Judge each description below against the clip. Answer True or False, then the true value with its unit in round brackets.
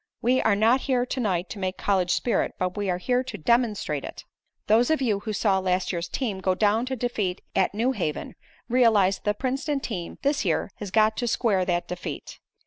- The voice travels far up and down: False (4.7 semitones)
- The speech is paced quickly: True (215 wpm)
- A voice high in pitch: True (210 Hz)